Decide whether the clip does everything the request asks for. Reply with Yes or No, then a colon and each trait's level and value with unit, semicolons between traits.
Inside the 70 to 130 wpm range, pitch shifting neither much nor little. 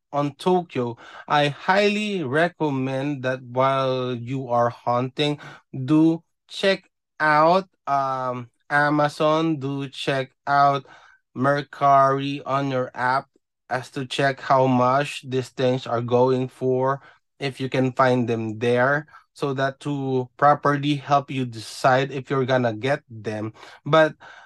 No: average, 125 wpm; narrow, 2.3 semitones